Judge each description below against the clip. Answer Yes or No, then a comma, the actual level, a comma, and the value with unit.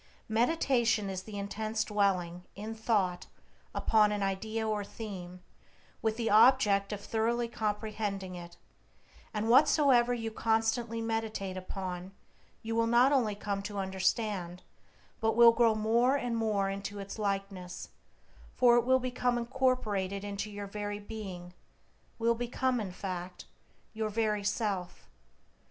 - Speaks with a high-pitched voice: Yes, high, 215 Hz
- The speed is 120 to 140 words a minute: Yes, slow, 135 wpm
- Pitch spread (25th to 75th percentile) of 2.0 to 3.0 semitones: Yes, narrow, 2.6 semitones